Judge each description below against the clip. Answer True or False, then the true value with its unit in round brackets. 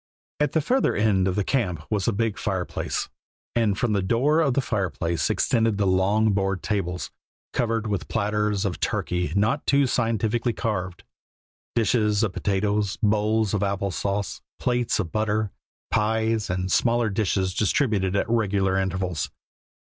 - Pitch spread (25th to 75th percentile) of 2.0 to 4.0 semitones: True (2.8 semitones)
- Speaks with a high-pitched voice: False (105 Hz)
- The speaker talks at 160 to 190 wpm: False (150 wpm)